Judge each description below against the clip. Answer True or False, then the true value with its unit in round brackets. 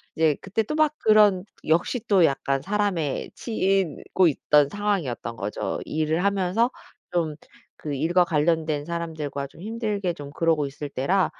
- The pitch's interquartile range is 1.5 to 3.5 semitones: False (5.1 semitones)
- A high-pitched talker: False (170 Hz)